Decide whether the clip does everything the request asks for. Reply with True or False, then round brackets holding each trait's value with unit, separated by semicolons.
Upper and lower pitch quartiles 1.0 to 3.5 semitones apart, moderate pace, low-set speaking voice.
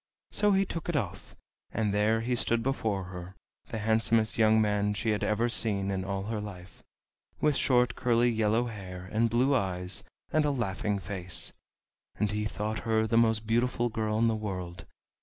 True (2.7 semitones; 180 wpm; 110 Hz)